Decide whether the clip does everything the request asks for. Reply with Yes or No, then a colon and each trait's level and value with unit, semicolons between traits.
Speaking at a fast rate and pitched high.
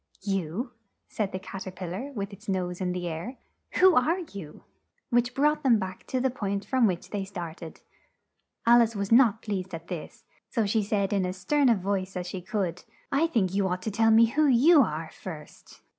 Yes: fast, 215 wpm; high, 200 Hz